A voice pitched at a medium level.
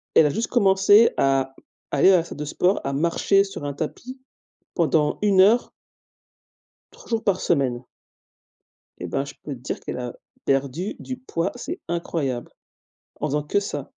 Yes: medium, 165 Hz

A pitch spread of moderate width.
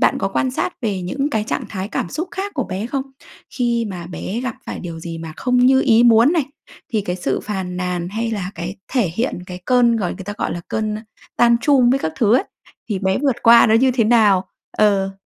Yes: average, 4.7 semitones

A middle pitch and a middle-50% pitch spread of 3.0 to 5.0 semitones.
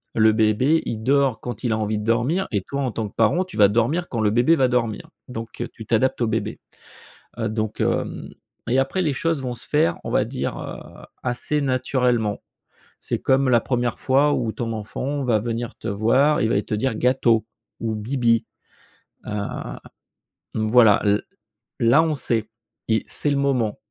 No: low, 120 Hz; average, 3.5 semitones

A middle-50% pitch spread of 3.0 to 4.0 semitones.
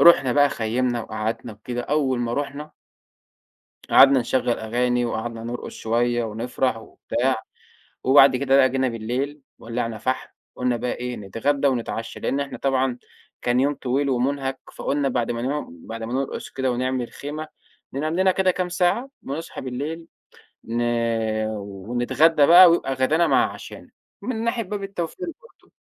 Yes: average, 3.5 semitones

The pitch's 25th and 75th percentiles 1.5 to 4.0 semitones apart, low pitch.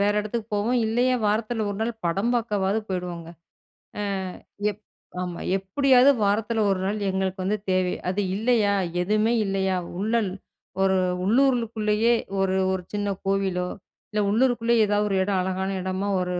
No: average, 2.9 semitones; high, 205 Hz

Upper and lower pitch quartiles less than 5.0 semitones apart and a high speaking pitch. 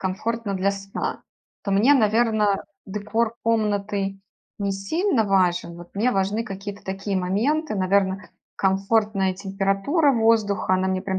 Yes: narrow, 2.5 semitones; high, 200 Hz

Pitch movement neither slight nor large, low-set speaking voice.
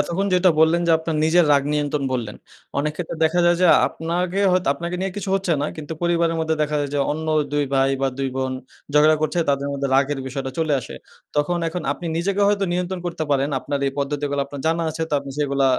No: average, 3.5 semitones; medium, 155 Hz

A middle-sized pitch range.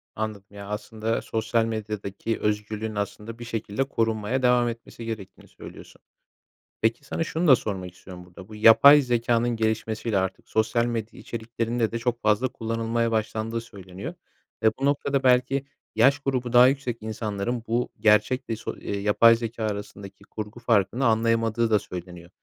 No: narrow, 2.2 semitones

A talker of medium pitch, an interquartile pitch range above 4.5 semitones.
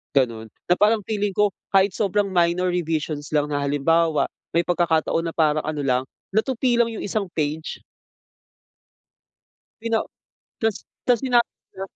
Yes: medium, 175 Hz; average, 5.3 semitones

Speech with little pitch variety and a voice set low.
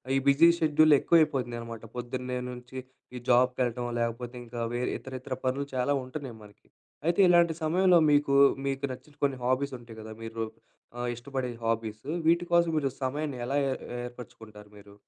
No: average, 3.3 semitones; low, 130 Hz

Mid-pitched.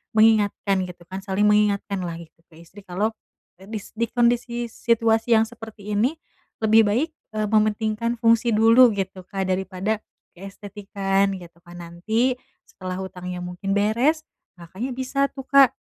No: high, 210 Hz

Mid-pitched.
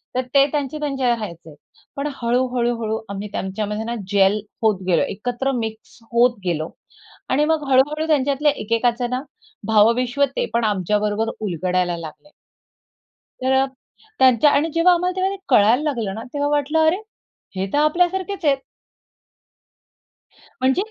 No: high, 245 Hz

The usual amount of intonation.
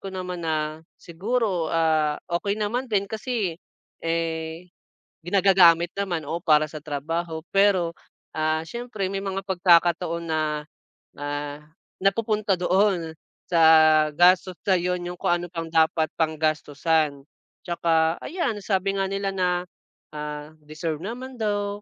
Yes: average, 3.6 semitones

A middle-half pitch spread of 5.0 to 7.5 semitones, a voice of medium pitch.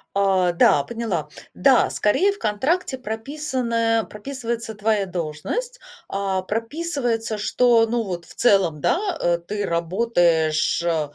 No: wide, 5.5 semitones; high, 215 Hz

